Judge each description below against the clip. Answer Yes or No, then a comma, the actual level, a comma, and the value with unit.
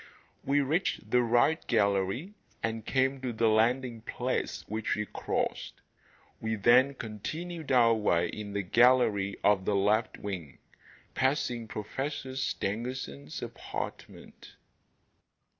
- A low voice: Yes, low, 115 Hz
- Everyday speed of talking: No, slow, 115 wpm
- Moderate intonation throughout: Yes, average, 4.0 semitones